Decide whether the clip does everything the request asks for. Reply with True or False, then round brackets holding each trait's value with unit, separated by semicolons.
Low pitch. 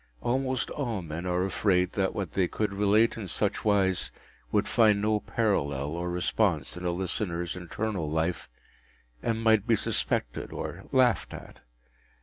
True (95 Hz)